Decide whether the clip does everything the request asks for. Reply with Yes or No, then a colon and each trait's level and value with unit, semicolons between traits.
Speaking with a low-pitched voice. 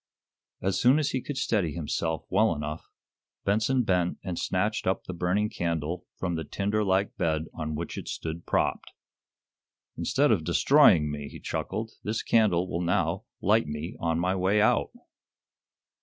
Yes: very low, 90 Hz